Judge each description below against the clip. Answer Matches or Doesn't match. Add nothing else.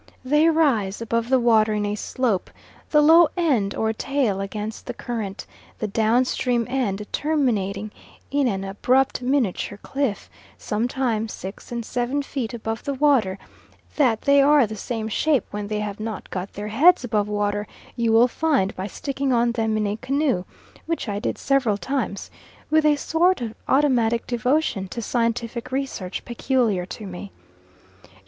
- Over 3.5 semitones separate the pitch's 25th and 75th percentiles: Matches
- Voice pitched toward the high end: Matches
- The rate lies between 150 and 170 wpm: Matches